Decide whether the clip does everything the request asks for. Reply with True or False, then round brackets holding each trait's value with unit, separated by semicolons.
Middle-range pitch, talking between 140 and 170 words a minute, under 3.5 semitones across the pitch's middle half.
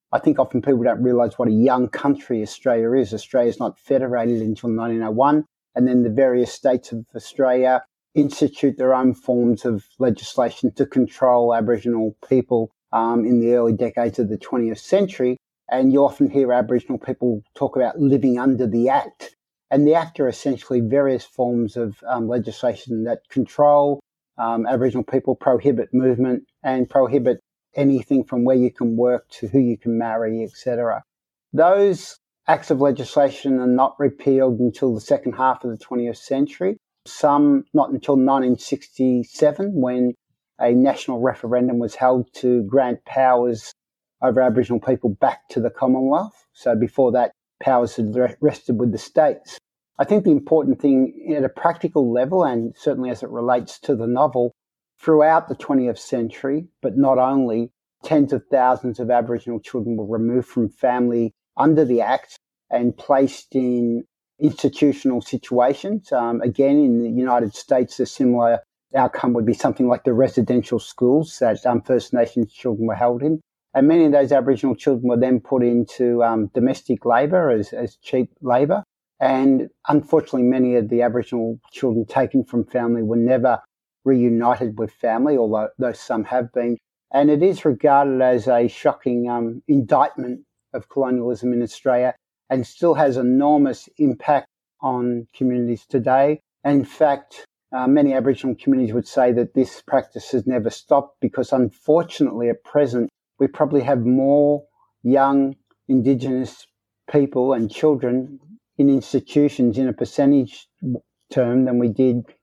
False (125 Hz; 155 wpm; 2.5 semitones)